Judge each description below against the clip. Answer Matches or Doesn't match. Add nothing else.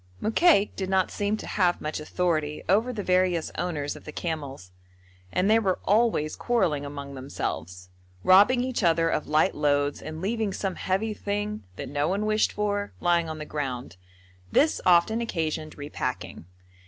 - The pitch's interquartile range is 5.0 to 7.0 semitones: Matches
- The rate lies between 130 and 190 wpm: Matches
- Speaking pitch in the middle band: Matches